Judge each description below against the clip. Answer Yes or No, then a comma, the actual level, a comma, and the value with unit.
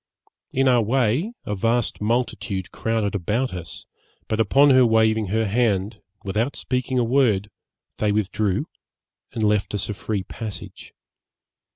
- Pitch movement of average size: Yes, average, 3.1 semitones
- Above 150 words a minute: No, average, 140 wpm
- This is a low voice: Yes, low, 110 Hz